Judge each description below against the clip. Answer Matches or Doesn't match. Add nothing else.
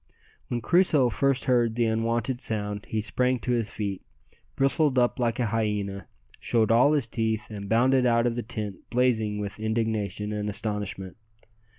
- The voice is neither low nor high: Doesn't match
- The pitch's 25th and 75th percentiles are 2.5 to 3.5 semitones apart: Matches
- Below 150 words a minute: Doesn't match